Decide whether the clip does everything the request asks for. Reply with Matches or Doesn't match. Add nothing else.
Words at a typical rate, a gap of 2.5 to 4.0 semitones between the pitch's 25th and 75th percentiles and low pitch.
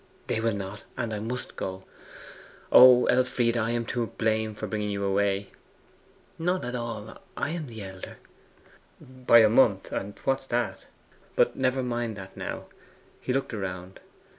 Matches